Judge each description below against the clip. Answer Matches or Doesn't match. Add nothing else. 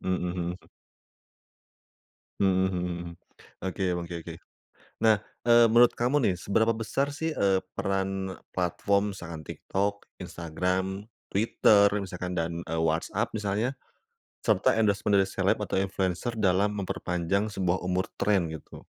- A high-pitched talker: Doesn't match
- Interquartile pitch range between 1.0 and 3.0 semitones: Matches